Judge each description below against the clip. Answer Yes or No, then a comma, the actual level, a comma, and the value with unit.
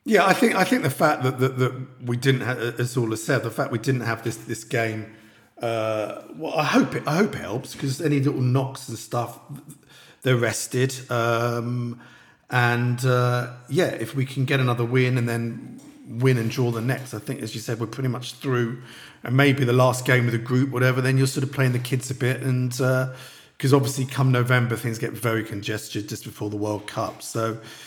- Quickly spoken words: Yes, fast, 220 wpm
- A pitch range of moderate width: No, narrow, 2.3 semitones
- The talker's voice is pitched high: No, low, 125 Hz